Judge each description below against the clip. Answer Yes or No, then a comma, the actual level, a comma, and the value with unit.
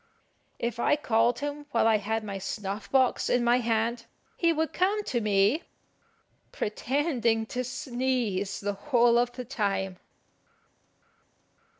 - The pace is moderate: No, slow, 130 wpm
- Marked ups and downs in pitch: No, average, 3.6 semitones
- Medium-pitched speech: No, high, 235 Hz